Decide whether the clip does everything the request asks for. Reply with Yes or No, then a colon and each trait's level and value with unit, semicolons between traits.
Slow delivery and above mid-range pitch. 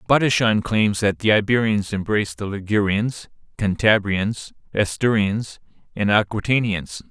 No: slow, 100 wpm; low, 105 Hz